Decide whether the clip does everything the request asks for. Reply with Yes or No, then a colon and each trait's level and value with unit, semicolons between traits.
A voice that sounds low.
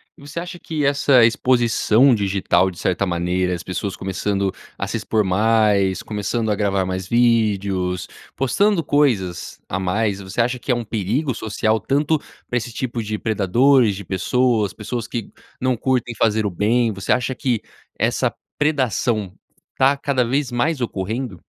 Yes: low, 110 Hz